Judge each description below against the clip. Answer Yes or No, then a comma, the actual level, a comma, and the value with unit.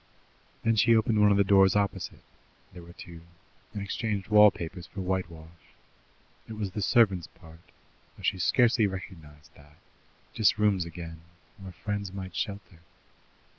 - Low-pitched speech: Yes, very low, 95 Hz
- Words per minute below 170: Yes, average, 150 wpm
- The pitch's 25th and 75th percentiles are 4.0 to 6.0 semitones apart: No, average, 3.3 semitones